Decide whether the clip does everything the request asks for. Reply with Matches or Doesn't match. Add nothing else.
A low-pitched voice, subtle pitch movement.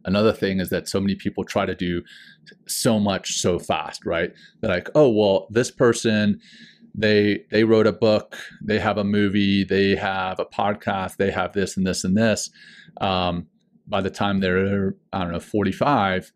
Matches